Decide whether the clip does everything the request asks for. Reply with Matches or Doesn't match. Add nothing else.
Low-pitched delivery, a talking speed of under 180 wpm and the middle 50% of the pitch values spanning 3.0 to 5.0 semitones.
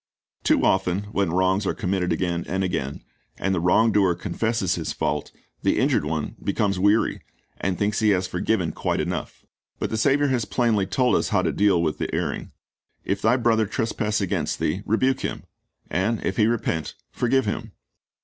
Doesn't match